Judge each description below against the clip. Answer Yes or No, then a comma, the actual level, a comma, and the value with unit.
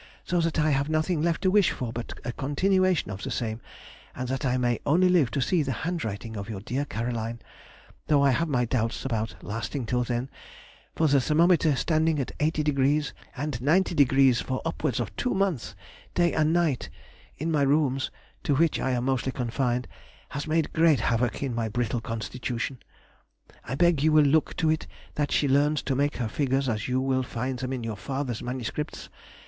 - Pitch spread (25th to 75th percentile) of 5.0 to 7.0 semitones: No, average, 4.3 semitones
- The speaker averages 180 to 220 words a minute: Yes, average, 190 wpm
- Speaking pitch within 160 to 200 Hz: No, low, 135 Hz